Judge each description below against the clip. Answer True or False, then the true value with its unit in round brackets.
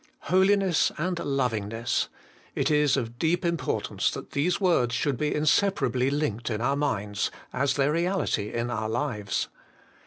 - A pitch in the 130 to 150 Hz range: True (140 Hz)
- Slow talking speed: False (150 wpm)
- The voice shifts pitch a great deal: True (5.8 semitones)